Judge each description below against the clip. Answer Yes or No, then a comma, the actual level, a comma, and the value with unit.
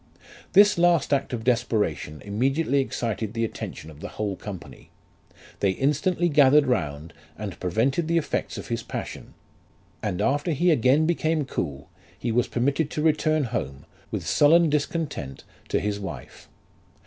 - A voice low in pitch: Yes, low, 130 Hz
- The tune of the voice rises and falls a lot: Yes, wide, 7.0 semitones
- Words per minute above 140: Yes, average, 150 wpm